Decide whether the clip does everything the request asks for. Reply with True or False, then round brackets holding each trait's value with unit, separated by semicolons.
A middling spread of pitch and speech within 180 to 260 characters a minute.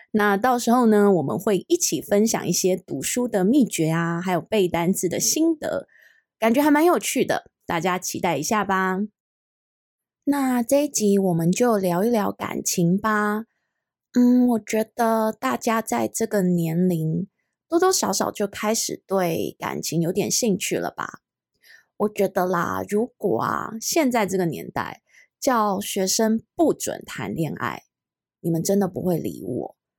True (4.7 semitones; 220 characters per minute)